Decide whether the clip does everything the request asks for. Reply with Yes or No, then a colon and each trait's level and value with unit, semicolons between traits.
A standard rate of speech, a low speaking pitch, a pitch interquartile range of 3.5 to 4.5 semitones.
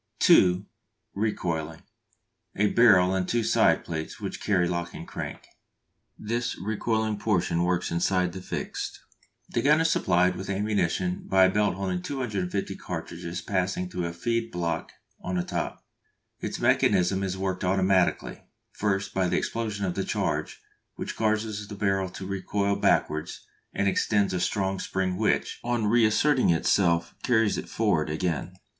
No: average, 150 wpm; very low, 95 Hz; average, 2.8 semitones